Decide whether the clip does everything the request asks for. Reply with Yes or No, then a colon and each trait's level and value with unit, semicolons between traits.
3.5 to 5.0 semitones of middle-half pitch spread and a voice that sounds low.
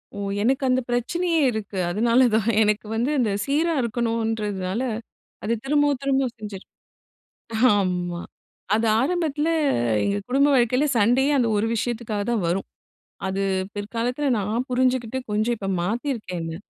No: average, 4.0 semitones; high, 235 Hz